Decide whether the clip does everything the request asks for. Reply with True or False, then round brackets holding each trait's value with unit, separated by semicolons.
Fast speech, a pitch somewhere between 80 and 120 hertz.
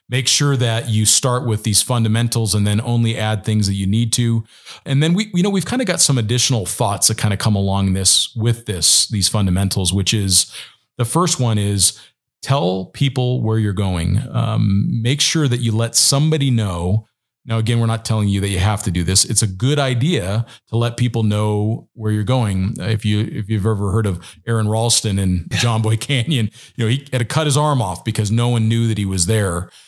True (225 wpm; 110 Hz)